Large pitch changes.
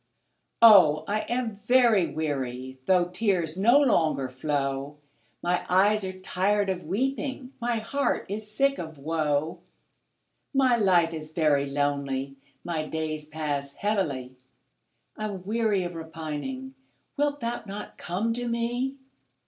Yes: wide, 6.8 semitones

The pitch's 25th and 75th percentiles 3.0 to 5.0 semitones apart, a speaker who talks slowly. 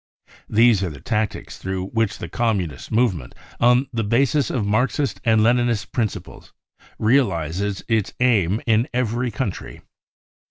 Yes: average, 3.5 semitones; slow, 130 wpm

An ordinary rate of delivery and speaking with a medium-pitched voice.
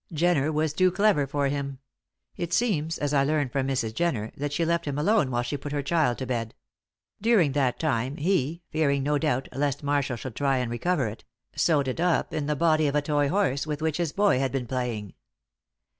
No: fast, 215 wpm; medium, 145 Hz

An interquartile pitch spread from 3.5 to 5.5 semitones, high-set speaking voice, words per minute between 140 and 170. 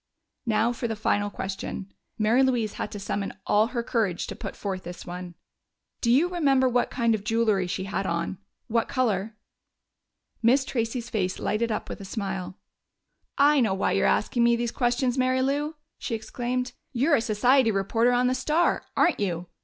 No: average, 4.0 semitones; high, 230 Hz; average, 180 wpm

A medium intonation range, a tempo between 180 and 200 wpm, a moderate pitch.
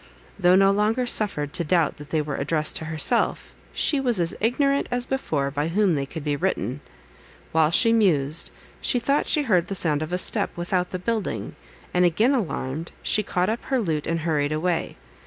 No: wide, 5.9 semitones; average, 195 wpm; medium, 175 Hz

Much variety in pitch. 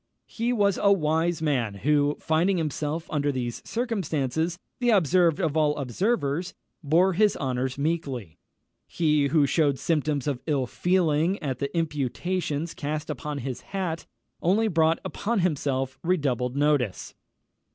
No: average, 4.0 semitones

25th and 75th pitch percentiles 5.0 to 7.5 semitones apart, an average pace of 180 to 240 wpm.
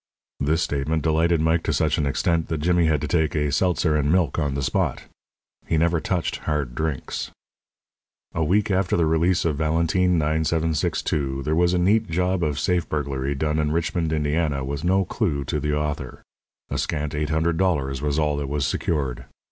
No: narrow, 2.6 semitones; average, 190 wpm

